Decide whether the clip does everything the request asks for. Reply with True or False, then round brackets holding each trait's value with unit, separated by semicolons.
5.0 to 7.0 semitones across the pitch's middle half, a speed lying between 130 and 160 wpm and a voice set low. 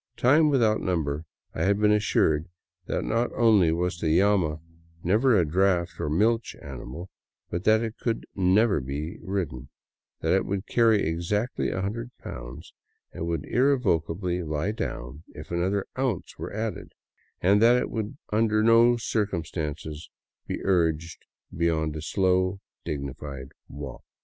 True (5.5 semitones; 145 wpm; 95 Hz)